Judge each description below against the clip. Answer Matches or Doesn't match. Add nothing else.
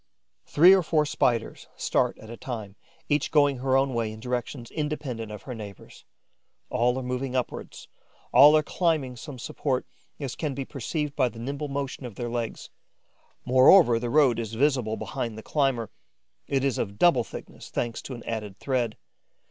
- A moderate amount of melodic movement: Matches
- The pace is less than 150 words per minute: Doesn't match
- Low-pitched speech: Matches